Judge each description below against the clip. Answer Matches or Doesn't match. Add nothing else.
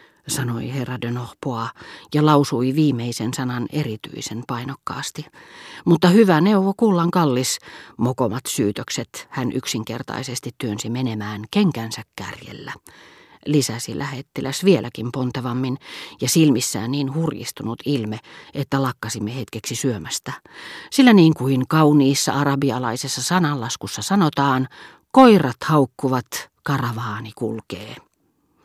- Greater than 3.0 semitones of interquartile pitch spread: Matches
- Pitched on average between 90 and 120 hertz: Doesn't match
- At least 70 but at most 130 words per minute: Matches